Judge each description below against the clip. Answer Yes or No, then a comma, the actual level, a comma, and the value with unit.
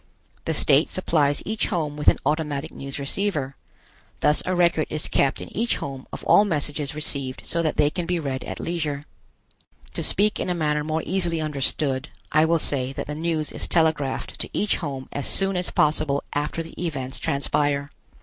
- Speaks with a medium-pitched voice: Yes, medium, 150 Hz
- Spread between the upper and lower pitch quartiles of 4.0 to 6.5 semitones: No, average, 3.0 semitones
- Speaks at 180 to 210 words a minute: Yes, average, 190 wpm